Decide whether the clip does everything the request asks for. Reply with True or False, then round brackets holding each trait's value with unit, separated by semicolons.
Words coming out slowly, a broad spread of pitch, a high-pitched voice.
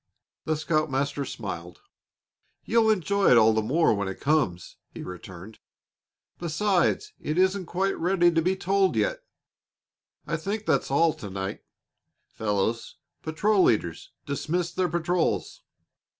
False (130 wpm; 8.5 semitones; 165 Hz)